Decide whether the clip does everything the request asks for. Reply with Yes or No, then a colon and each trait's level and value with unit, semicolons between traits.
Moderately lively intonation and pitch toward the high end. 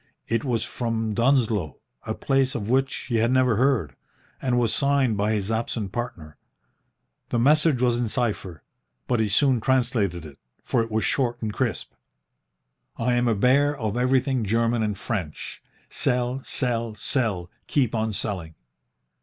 No: average, 3.2 semitones; low, 115 Hz